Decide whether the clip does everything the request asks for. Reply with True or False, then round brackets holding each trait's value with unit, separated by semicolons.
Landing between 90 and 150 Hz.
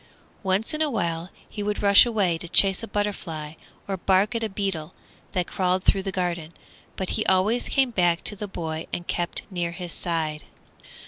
False (185 Hz)